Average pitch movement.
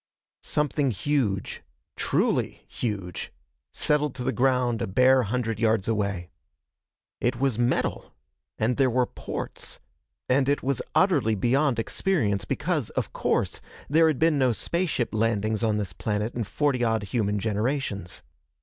Yes: average, 4.5 semitones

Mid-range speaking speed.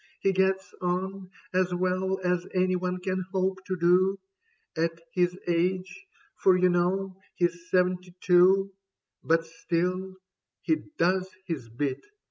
No: slow, 130 wpm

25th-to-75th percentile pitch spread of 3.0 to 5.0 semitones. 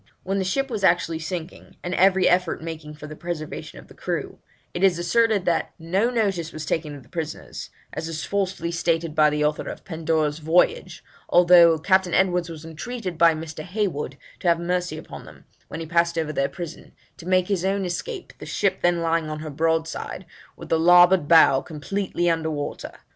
No: narrow, 2.6 semitones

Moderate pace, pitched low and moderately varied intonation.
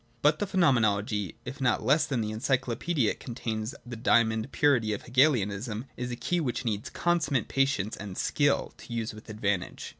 Yes: average, 175 wpm; low, 120 Hz; average, 4.1 semitones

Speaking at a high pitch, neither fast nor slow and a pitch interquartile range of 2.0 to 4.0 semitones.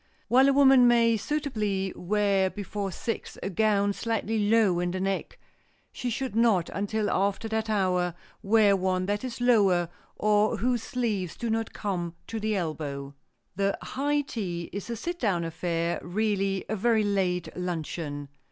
Yes: high, 205 Hz; average, 160 wpm; average, 3.7 semitones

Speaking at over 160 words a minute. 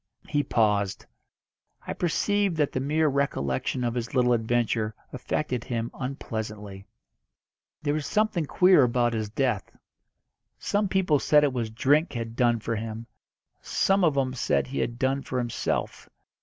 No: average, 150 wpm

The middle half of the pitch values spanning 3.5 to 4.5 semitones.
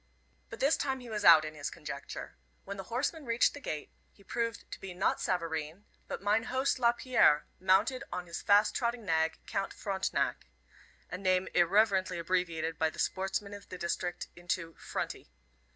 No: average, 5.0 semitones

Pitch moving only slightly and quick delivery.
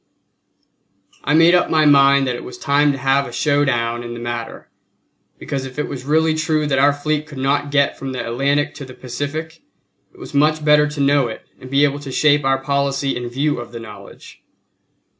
Yes: narrow, 2.2 semitones; fast, 215 wpm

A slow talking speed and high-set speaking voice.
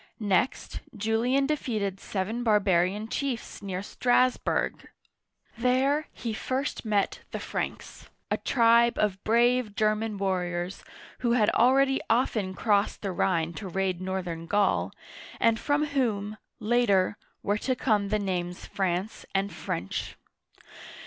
Yes: slow, 125 wpm; high, 210 Hz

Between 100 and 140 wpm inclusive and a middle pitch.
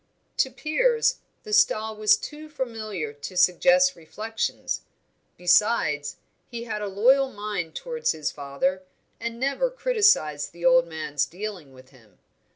No: slow, 135 wpm; high, 210 Hz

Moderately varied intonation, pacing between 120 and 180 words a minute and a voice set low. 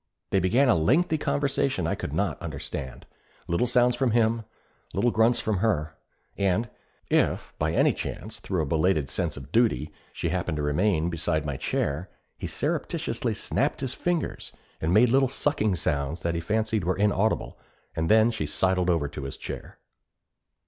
No: wide, 6.7 semitones; average, 165 wpm; very low, 95 Hz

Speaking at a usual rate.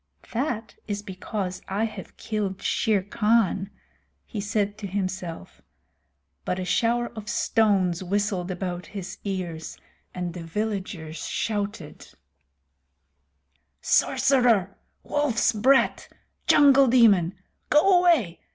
No: slow, 105 wpm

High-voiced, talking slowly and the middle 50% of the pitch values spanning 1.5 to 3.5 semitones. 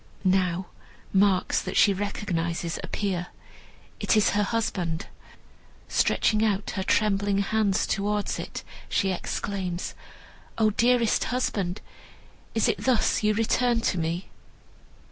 Yes: high, 200 Hz; slow, 115 wpm; narrow, 2.6 semitones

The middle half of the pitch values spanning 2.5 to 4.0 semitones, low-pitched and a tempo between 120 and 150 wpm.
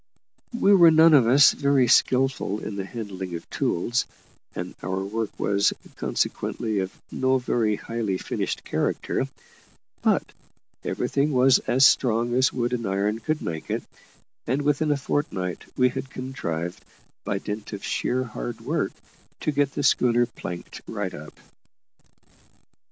No: average, 5.1 semitones; low, 120 Hz; average, 145 wpm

